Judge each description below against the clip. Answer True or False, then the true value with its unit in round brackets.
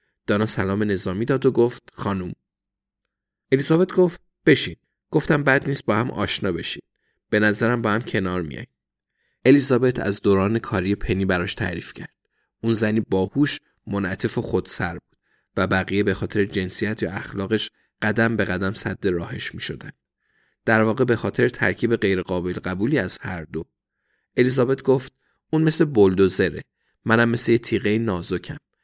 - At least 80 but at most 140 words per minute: False (150 wpm)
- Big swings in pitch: False (4.4 semitones)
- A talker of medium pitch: False (110 Hz)